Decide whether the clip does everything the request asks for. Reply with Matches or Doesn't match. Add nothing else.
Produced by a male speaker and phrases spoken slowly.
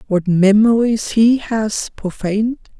Doesn't match